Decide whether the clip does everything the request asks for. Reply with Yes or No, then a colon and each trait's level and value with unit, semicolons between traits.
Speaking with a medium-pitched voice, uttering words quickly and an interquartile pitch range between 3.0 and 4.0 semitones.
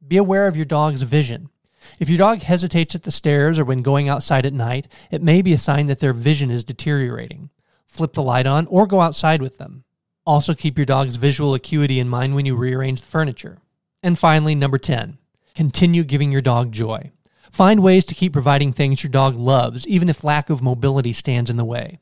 Yes: medium, 145 Hz; fast, 215 wpm; average, 3.5 semitones